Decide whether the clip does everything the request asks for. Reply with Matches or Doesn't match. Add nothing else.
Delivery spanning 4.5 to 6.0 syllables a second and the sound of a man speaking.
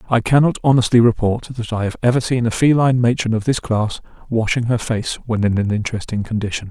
Doesn't match